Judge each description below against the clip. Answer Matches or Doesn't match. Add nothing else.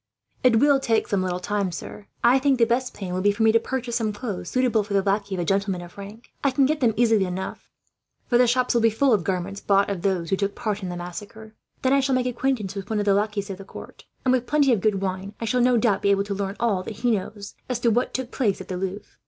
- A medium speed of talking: Doesn't match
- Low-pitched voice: Doesn't match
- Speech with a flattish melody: Doesn't match